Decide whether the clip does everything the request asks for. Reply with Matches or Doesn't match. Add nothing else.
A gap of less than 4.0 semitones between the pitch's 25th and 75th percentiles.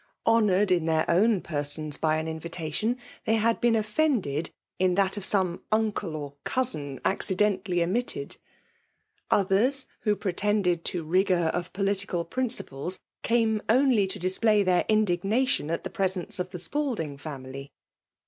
Doesn't match